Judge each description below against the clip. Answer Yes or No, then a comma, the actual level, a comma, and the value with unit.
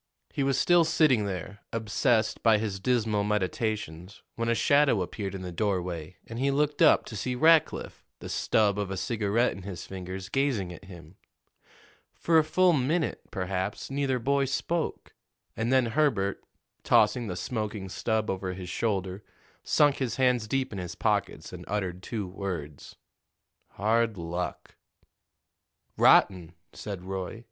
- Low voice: Yes, low, 105 Hz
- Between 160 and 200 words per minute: No, average, 150 wpm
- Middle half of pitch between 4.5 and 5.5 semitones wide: Yes, average, 5.2 semitones